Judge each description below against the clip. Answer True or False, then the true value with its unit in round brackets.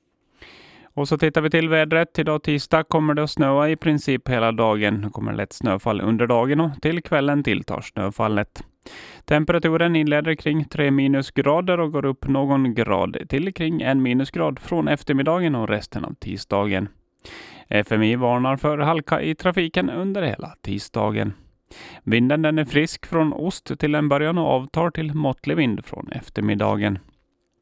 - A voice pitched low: False (145 Hz)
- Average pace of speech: True (160 wpm)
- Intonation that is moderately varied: False (6.3 semitones)